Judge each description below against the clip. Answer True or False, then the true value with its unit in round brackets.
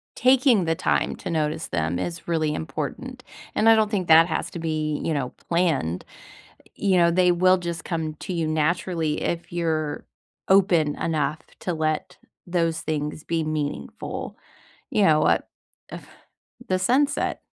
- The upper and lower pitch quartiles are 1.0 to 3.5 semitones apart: True (2.8 semitones)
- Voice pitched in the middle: True (165 Hz)